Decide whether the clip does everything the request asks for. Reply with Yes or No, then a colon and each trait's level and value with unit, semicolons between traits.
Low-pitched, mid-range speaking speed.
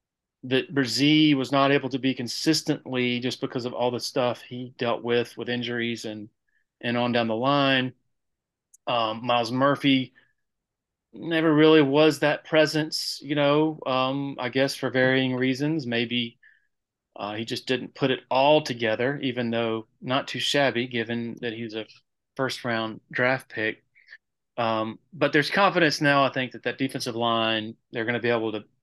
Yes: low, 125 Hz; average, 170 wpm